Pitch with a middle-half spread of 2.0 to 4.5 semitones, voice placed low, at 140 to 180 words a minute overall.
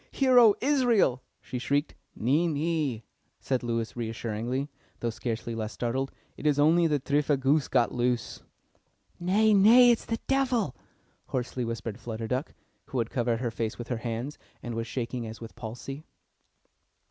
No: wide, 5.4 semitones; low, 130 Hz; average, 160 wpm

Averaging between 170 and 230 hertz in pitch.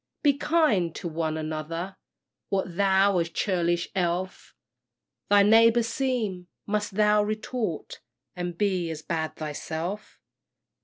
Yes: high, 190 Hz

